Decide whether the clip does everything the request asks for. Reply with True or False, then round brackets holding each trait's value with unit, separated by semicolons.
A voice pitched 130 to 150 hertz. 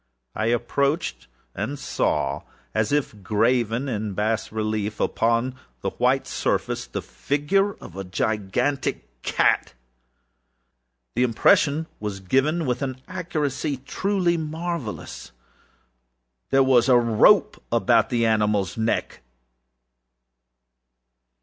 False (120 Hz)